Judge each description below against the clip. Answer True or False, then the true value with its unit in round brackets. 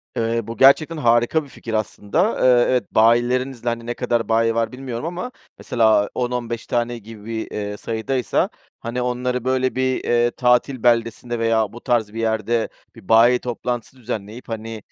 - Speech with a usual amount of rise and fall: False (1.8 semitones)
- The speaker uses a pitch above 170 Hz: False (120 Hz)